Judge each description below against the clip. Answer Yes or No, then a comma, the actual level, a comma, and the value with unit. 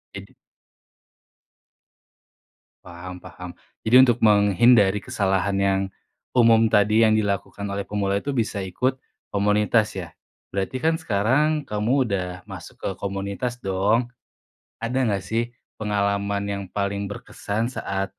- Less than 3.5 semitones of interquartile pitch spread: Yes, average, 2.7 semitones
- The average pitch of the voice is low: Yes, low, 105 Hz